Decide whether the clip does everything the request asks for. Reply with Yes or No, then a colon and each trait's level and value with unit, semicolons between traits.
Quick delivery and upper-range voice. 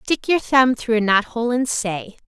Yes: fast, 210 wpm; high, 235 Hz